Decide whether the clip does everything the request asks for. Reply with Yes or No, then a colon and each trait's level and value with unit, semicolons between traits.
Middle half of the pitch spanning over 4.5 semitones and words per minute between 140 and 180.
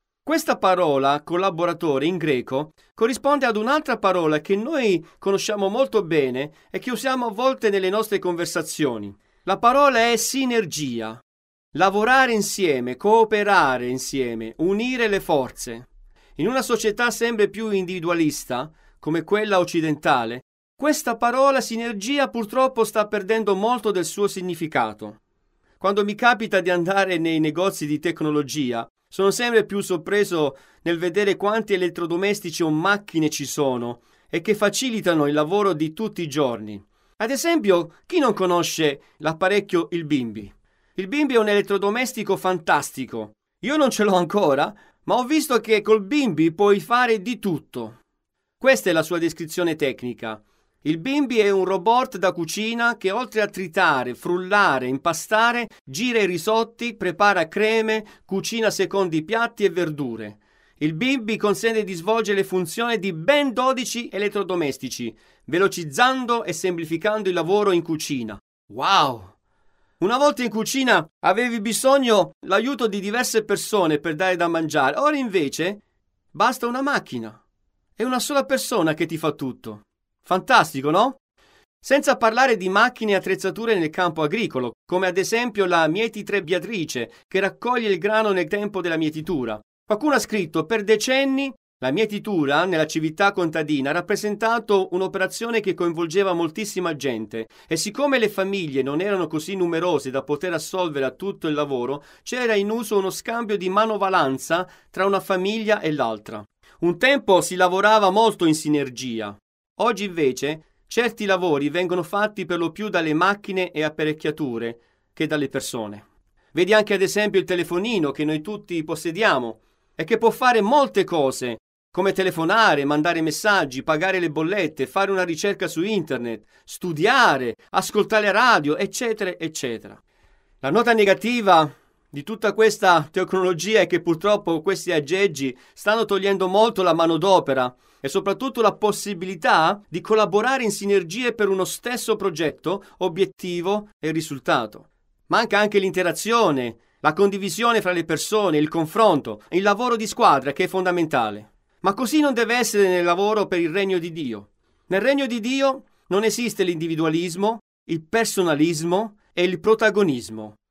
Yes: wide, 5.6 semitones; average, 145 wpm